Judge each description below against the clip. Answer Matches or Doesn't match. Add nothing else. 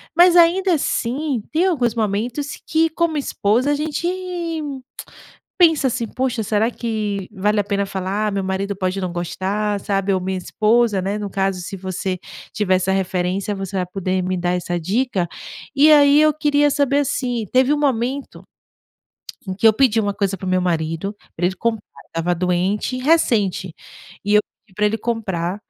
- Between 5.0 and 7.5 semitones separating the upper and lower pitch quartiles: Matches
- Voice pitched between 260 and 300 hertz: Doesn't match